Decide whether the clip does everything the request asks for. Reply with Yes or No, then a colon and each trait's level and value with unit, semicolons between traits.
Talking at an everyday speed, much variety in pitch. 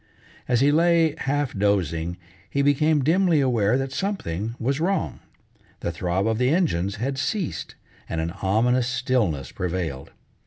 Yes: average, 145 wpm; wide, 7.5 semitones